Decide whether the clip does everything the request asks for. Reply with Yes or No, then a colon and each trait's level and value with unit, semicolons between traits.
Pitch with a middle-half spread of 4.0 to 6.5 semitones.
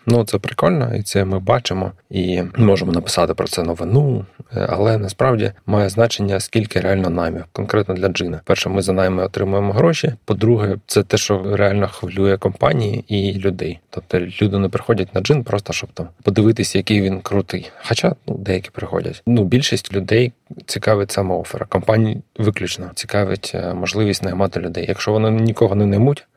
No: average, 3.0 semitones